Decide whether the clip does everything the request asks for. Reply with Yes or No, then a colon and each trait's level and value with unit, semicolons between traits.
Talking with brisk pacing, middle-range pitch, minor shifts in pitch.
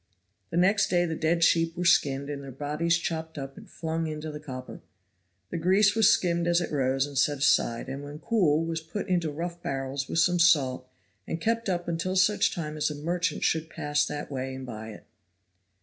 No: fast, 210 wpm; medium, 160 Hz; average, 3.5 semitones